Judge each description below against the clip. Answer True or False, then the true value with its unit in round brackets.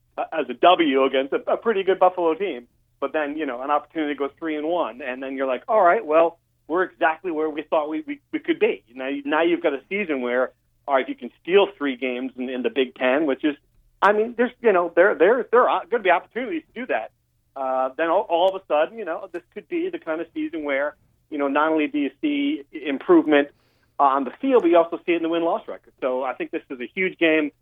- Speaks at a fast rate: True (260 wpm)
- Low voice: False (155 Hz)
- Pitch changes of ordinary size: False (5.7 semitones)